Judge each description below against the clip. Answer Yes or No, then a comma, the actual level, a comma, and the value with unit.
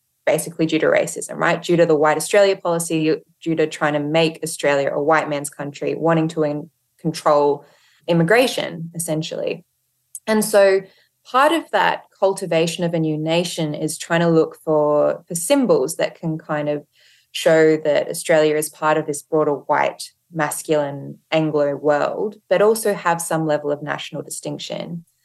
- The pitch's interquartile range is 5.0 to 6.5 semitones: No, narrow, 2.5 semitones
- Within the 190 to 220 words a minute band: No, average, 160 wpm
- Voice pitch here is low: No, medium, 160 Hz